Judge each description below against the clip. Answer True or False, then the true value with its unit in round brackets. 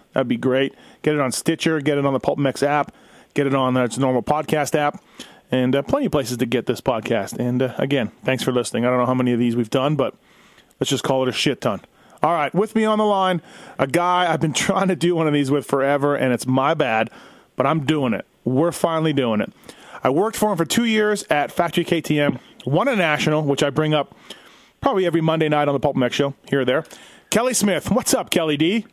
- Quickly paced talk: True (250 wpm)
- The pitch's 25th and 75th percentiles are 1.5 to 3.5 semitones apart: False (4.7 semitones)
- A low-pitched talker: False (145 Hz)